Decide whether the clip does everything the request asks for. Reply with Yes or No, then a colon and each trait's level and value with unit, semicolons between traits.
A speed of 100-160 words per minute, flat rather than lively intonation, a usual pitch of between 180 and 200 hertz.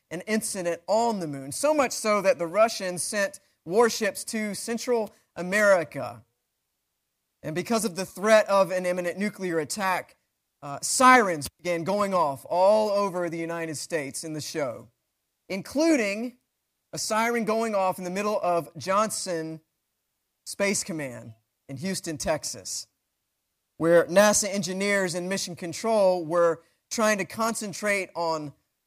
No: slow, 135 wpm; average, 4.3 semitones; high, 190 Hz